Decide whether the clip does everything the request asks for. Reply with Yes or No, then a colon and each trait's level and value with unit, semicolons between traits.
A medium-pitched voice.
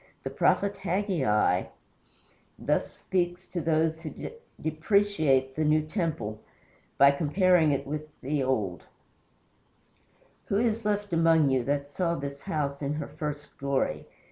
Yes: medium, 155 Hz